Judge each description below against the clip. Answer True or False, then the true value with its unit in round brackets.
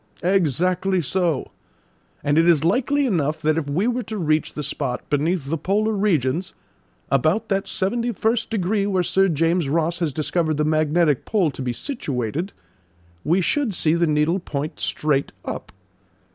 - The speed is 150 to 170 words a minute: True (160 wpm)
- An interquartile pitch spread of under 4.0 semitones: False (4.4 semitones)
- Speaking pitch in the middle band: True (170 Hz)